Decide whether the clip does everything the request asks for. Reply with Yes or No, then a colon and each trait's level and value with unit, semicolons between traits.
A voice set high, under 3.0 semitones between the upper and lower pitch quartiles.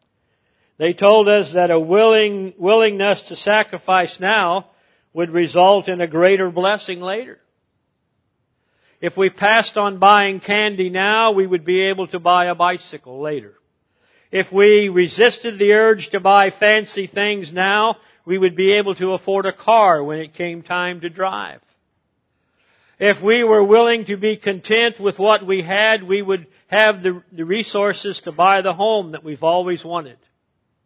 Yes: high, 195 Hz; narrow, 2.5 semitones